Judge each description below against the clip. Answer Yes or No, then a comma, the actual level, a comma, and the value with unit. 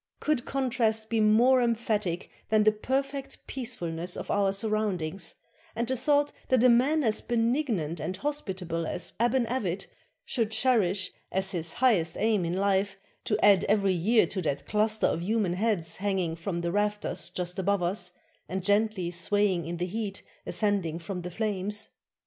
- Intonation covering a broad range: No, average, 4.2 semitones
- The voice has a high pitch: Yes, high, 205 Hz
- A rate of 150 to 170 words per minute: Yes, average, 160 wpm